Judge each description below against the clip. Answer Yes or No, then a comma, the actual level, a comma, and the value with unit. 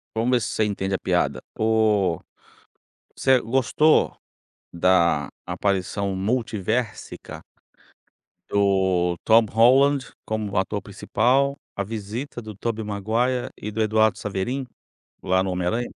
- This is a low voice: Yes, low, 110 Hz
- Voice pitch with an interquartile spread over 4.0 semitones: No, average, 3.6 semitones